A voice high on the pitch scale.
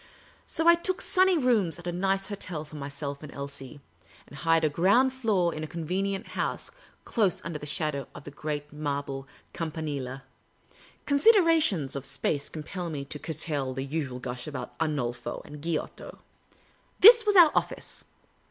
No: medium, 155 Hz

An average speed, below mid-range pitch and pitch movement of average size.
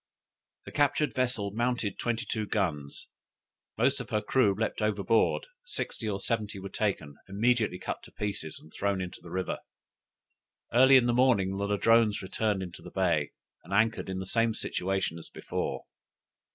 Yes: average, 165 wpm; low, 105 Hz; average, 3.5 semitones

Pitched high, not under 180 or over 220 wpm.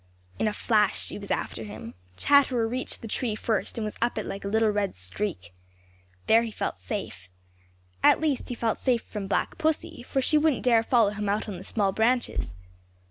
Yes: high, 220 Hz; average, 200 wpm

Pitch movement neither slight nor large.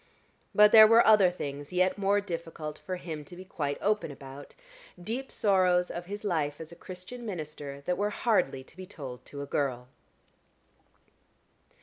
No: wide, 5.8 semitones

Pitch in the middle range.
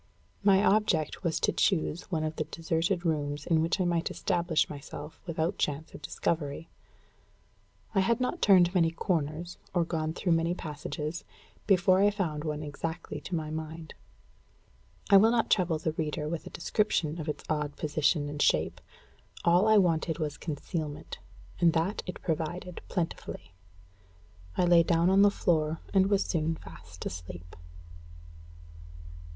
Yes: medium, 165 Hz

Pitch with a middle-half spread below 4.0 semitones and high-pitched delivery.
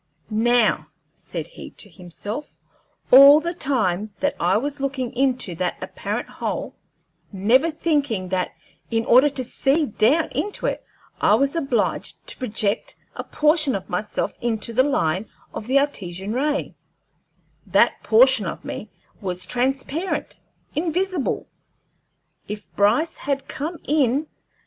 No: wide, 5.6 semitones; very high, 255 Hz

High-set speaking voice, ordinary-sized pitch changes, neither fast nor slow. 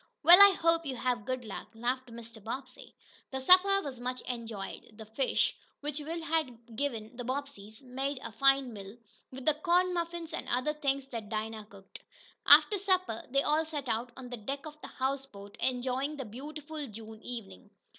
Yes: very high, 260 Hz; average, 4.8 semitones; average, 175 wpm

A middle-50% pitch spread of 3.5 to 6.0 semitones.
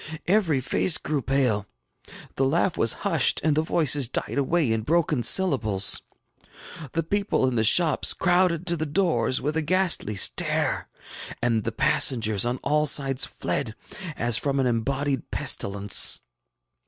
Yes: wide, 5.6 semitones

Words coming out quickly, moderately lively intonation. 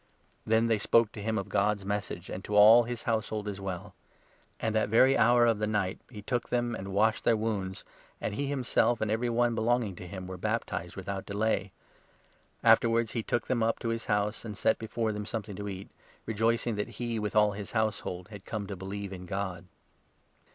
No: fast, 215 wpm; narrow, 2.3 semitones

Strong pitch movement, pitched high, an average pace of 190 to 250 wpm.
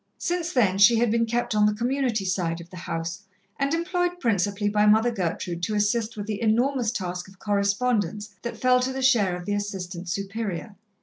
No: average, 3.8 semitones; high, 210 Hz; average, 195 wpm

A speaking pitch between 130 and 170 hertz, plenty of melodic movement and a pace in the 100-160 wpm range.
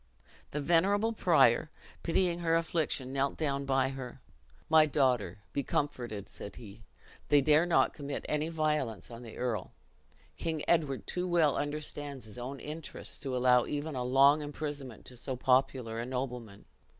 No: medium, 140 Hz; average, 3.7 semitones; average, 155 wpm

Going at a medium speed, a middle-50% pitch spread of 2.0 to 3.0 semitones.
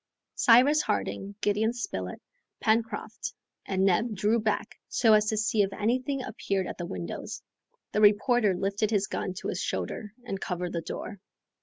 Yes: average, 160 wpm; average, 2.7 semitones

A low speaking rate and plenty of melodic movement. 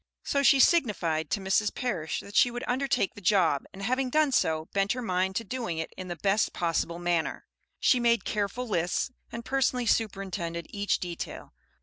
No: average, 185 wpm; wide, 5.9 semitones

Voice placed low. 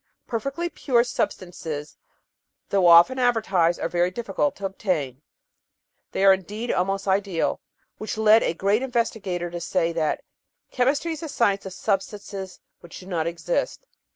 No: high, 195 Hz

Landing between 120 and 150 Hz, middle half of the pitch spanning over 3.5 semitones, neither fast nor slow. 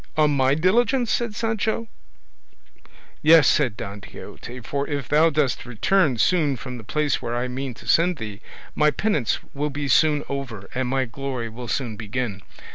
Yes: medium, 140 Hz; average, 4.2 semitones; average, 170 wpm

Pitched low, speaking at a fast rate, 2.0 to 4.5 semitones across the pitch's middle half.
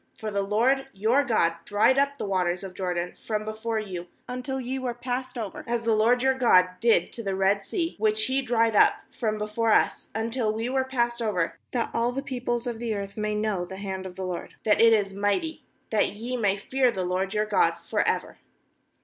No: high, 220 Hz; fast, 215 wpm; average, 3.7 semitones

